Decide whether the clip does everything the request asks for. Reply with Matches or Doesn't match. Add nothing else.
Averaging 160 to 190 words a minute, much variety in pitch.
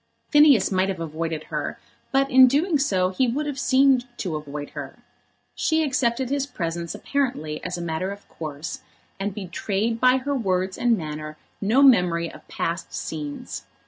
Matches